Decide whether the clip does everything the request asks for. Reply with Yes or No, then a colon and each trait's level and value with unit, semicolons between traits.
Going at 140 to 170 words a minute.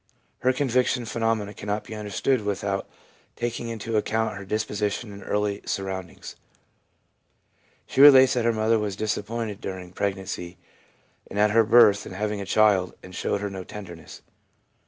Yes: average, 155 wpm